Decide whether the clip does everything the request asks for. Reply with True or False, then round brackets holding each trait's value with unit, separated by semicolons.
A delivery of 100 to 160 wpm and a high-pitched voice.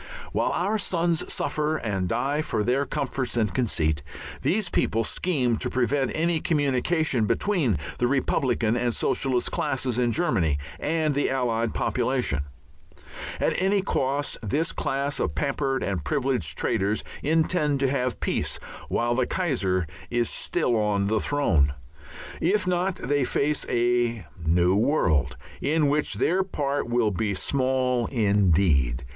False (140 wpm; 130 Hz)